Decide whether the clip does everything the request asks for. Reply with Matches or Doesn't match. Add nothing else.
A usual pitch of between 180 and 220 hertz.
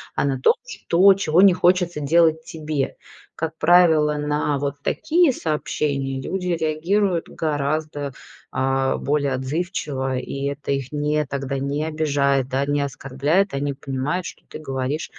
Doesn't match